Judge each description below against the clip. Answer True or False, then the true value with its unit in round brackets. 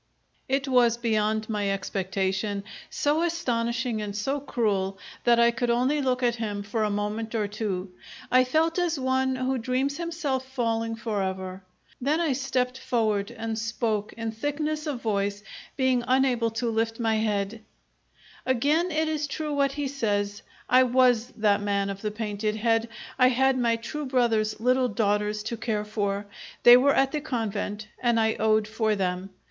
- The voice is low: False (230 Hz)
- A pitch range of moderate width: True (3.7 semitones)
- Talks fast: False (165 wpm)